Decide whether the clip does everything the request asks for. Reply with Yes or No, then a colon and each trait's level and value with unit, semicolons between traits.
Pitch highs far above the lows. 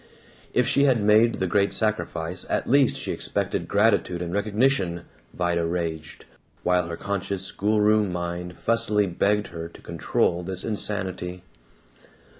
No: average, 3.4 semitones